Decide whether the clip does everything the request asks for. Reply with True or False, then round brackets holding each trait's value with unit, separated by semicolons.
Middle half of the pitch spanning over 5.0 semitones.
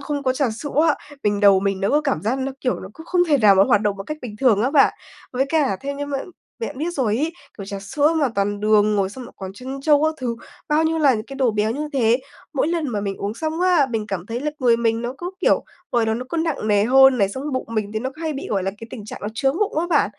True (5.6 semitones)